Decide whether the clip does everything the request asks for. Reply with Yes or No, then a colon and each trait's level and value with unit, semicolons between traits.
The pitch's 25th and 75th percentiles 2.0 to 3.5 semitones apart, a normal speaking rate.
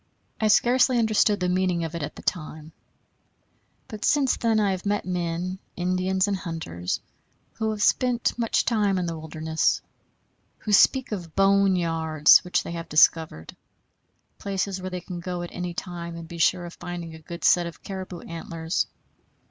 Yes: average, 3.0 semitones; average, 170 wpm